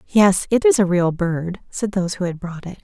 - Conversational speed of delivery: No, fast, 255 wpm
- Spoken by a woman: Yes, female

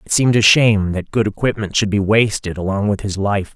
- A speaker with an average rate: No, fast, 235 wpm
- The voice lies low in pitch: Yes, low, 105 Hz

